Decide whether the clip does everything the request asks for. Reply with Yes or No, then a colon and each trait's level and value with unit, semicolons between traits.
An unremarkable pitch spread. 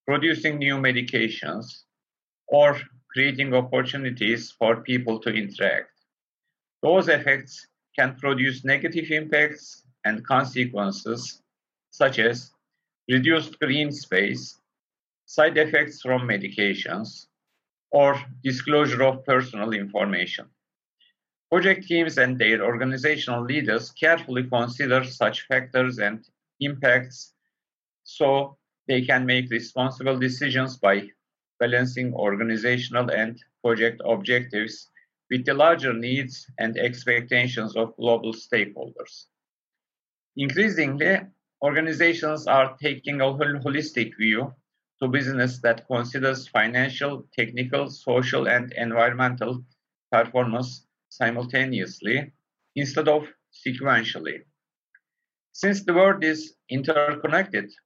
Yes: average, 3.2 semitones